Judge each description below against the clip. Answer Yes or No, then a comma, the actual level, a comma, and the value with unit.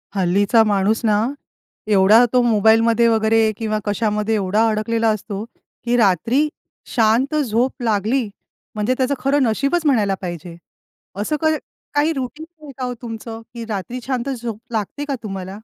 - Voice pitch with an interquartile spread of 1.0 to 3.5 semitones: Yes, average, 3.2 semitones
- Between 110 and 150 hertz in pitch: No, high, 225 Hz